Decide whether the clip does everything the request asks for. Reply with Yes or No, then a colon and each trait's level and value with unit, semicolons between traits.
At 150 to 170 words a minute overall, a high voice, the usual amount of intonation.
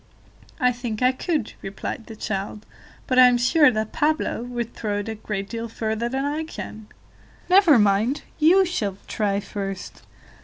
Yes: average, 165 wpm; high, 235 Hz; average, 4.2 semitones